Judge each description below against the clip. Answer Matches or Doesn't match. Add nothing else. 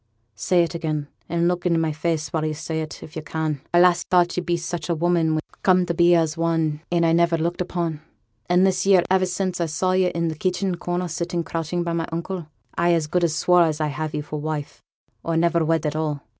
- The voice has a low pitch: Doesn't match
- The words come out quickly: Matches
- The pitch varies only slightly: Matches